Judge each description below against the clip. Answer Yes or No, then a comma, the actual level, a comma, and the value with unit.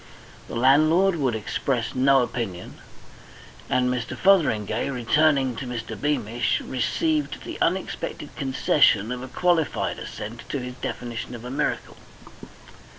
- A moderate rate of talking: No, slow, 125 wpm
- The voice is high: No, low, 125 Hz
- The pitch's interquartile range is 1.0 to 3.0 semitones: No, average, 3.7 semitones